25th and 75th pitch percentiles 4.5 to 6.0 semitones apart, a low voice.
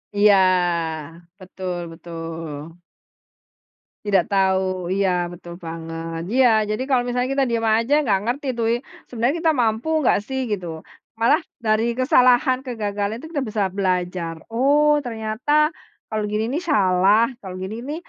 No: average, 5.2 semitones; high, 215 Hz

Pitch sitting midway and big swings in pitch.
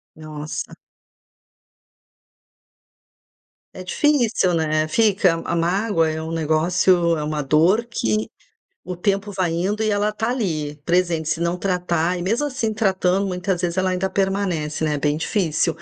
No: medium, 180 Hz; average, 3.8 semitones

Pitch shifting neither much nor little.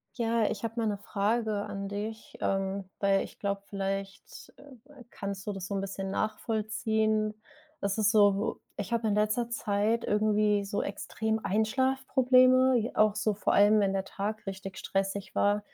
No: narrow, 1.8 semitones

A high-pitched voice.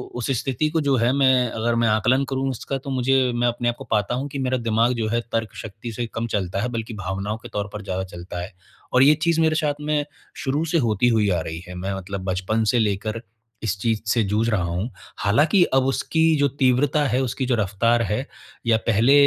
No: low, 115 Hz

